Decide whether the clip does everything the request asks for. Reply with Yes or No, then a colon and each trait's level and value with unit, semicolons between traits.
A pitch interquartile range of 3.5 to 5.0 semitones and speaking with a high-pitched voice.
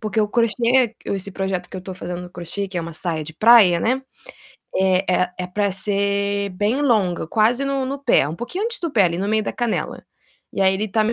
Yes: average, 4.2 semitones; high, 200 Hz